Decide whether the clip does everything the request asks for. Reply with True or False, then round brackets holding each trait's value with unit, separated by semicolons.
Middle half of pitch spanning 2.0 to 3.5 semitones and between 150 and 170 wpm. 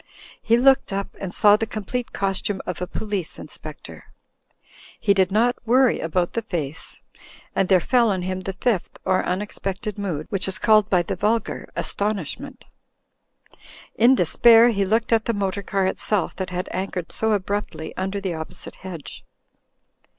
True (2.9 semitones; 165 wpm)